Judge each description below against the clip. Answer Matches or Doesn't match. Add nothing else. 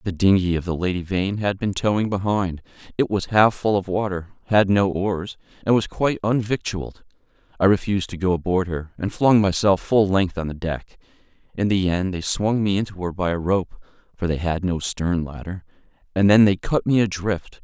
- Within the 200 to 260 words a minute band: Matches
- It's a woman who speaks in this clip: Doesn't match